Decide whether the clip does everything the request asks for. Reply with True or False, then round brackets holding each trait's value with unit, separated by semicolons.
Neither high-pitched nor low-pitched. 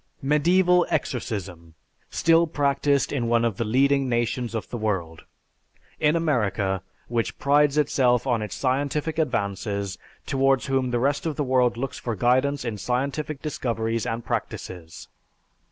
False (125 Hz)